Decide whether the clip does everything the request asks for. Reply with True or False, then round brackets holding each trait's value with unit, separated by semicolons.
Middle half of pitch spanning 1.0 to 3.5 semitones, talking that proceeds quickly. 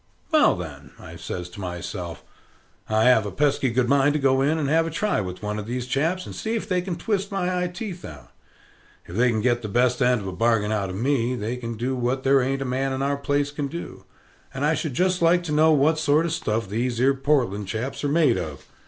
False (5.2 semitones; 250 wpm)